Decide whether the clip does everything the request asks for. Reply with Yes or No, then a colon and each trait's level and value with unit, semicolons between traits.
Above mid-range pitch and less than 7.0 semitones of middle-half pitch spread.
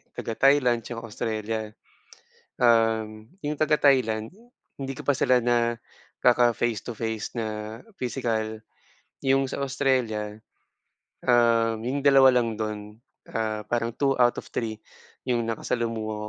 No: low, 115 Hz; narrow, 2.4 semitones